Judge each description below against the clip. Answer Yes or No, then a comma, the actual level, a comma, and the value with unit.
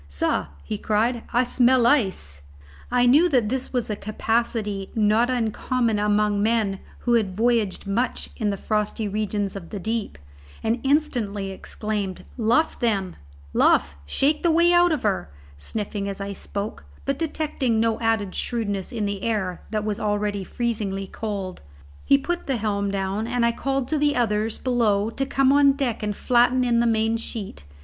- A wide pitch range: No, average, 3.4 semitones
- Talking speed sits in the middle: Yes, average, 170 wpm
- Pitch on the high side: Yes, high, 220 Hz